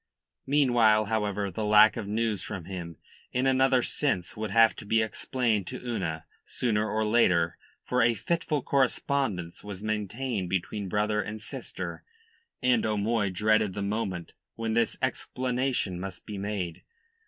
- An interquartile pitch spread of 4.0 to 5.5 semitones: No, average, 3.2 semitones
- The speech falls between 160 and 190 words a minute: No, average, 145 wpm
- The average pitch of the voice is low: Yes, low, 110 Hz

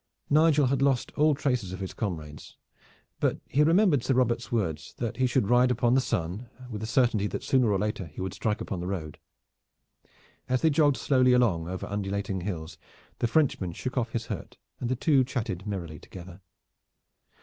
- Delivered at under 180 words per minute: No, average, 185 wpm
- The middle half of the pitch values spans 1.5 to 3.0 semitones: No, wide, 5.4 semitones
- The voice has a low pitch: Yes, low, 115 Hz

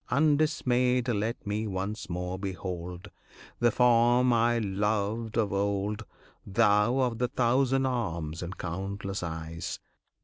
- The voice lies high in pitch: No, low, 105 Hz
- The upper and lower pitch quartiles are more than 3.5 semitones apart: Yes, average, 4.2 semitones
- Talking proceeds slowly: Yes, slow, 115 wpm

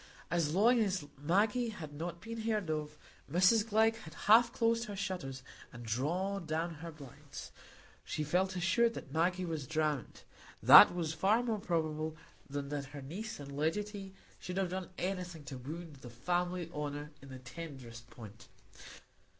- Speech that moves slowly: No, average, 160 wpm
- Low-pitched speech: No, medium, 170 Hz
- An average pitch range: Yes, average, 4.9 semitones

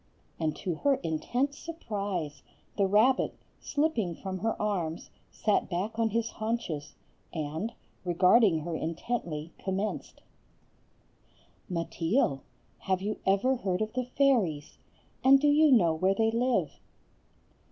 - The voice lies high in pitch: Yes, high, 200 Hz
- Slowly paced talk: Yes, slow, 120 wpm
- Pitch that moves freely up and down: Yes, wide, 5.9 semitones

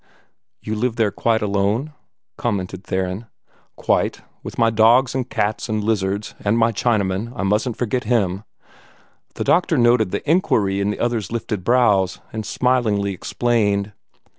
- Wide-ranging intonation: No, average, 3.1 semitones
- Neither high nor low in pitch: No, low, 110 Hz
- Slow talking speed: No, average, 145 wpm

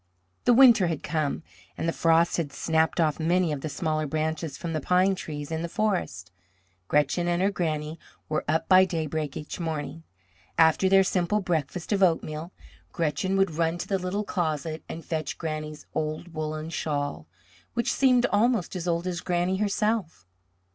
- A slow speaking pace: No, average, 170 wpm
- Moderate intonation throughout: Yes, average, 3.0 semitones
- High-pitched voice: No, medium, 165 Hz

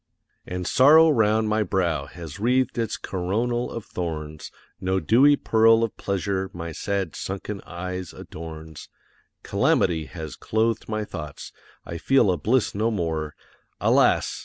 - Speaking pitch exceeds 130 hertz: No, very low, 95 Hz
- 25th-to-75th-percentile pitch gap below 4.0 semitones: No, average, 5.1 semitones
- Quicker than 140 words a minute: No, slow, 135 wpm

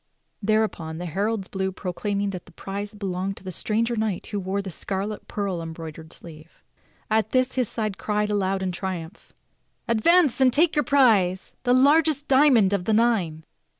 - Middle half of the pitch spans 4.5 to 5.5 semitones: No, average, 3.8 semitones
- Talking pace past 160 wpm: Yes, average, 175 wpm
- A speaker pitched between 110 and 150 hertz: No, high, 205 Hz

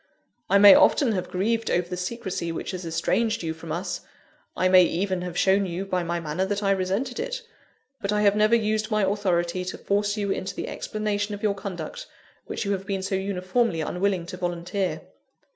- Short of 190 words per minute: No, average, 200 wpm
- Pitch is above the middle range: Yes, high, 195 Hz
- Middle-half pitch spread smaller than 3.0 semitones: Yes, narrow, 2.6 semitones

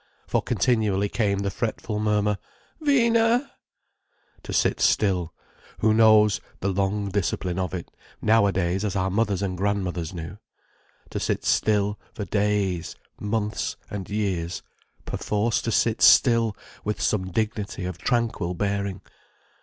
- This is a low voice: Yes, low, 100 Hz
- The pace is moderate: No, slow, 120 wpm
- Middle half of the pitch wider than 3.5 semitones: No, narrow, 2.4 semitones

